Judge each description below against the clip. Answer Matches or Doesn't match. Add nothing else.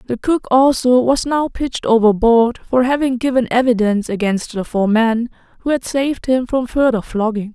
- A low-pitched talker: Doesn't match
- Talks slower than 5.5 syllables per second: Matches